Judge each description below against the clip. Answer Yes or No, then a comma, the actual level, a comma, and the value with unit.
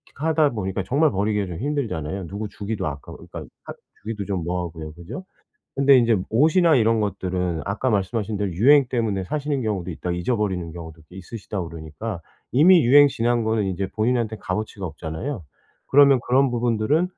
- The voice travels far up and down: Yes, wide, 5.7 semitones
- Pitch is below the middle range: Yes, low, 105 Hz